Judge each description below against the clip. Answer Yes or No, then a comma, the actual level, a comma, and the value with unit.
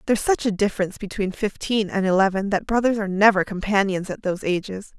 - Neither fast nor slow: Yes, average, 195 wpm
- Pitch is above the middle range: Yes, high, 200 Hz